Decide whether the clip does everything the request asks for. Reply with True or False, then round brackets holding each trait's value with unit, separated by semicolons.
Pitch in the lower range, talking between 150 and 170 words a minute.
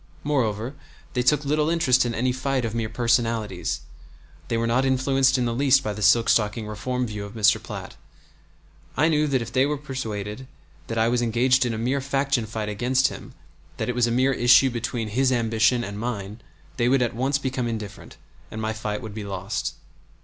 False (120 Hz; 200 wpm)